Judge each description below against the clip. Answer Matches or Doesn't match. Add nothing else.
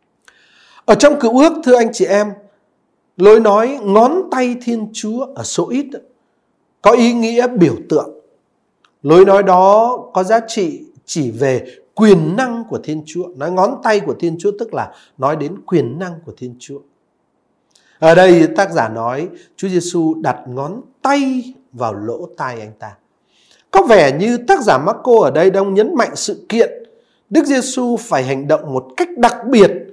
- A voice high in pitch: Matches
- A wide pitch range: Matches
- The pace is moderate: Matches